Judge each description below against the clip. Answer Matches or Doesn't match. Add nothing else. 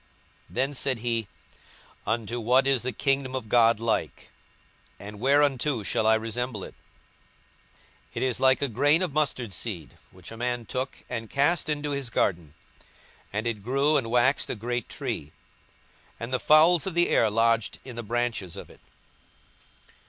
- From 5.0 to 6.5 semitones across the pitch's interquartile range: Doesn't match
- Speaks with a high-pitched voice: Doesn't match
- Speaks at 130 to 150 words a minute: Doesn't match